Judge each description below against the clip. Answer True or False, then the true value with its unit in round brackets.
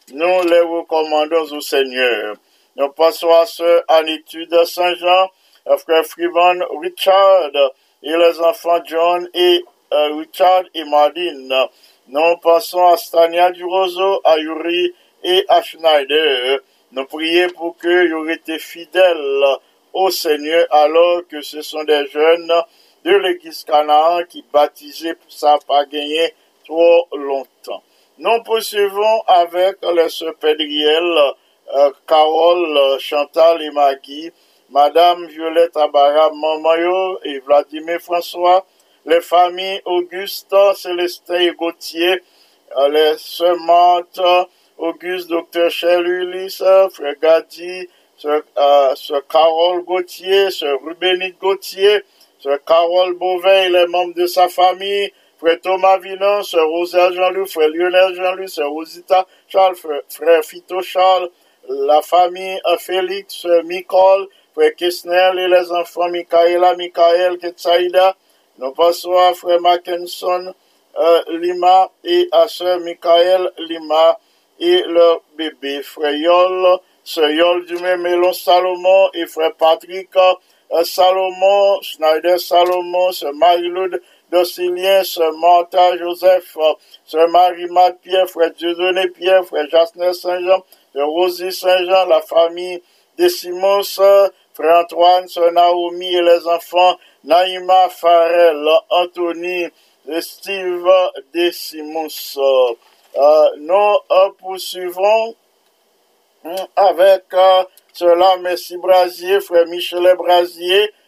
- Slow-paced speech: True (115 wpm)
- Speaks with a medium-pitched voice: True (175 Hz)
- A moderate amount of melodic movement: False (2.2 semitones)